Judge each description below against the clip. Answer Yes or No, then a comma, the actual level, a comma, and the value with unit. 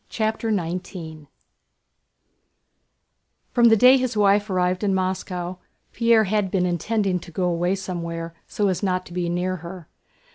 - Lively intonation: No, average, 3.0 semitones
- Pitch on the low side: No, medium, 185 Hz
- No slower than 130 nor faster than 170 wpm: Yes, average, 145 wpm